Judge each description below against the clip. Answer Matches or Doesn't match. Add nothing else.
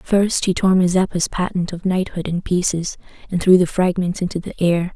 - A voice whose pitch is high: Doesn't match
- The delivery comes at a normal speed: Matches